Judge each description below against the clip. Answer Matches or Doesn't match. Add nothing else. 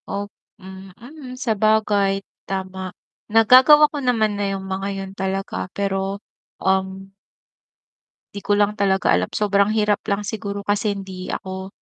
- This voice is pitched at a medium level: Doesn't match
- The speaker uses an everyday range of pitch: Doesn't match